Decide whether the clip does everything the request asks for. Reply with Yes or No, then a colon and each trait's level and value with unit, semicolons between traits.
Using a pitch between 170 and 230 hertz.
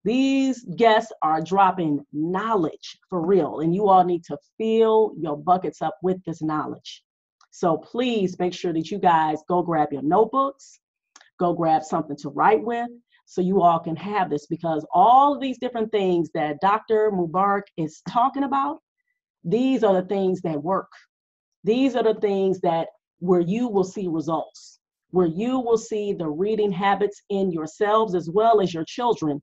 Yes: high, 190 Hz